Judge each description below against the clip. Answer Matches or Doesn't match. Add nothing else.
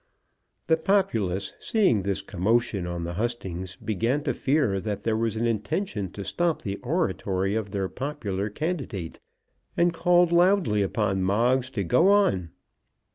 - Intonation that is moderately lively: Doesn't match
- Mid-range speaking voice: Doesn't match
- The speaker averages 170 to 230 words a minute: Doesn't match